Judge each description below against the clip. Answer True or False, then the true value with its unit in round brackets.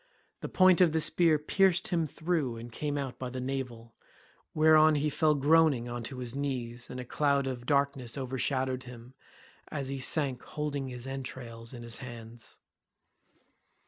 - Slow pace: False (165 wpm)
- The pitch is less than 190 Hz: True (135 Hz)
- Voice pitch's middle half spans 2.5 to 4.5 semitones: True (3.5 semitones)